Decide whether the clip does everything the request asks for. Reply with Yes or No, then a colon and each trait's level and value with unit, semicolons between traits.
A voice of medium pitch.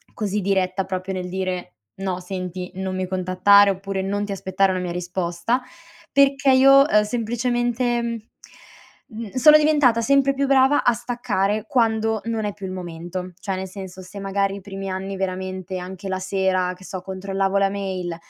No: high, 195 Hz